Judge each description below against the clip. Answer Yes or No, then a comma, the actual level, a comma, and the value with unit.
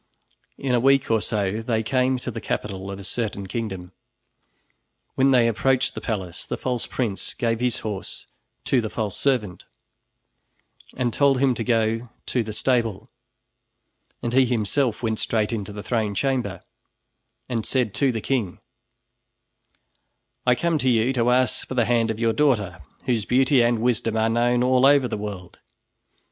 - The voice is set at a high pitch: No, low, 115 Hz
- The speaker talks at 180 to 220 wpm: No, average, 165 wpm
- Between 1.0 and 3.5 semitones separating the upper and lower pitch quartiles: Yes, average, 3.0 semitones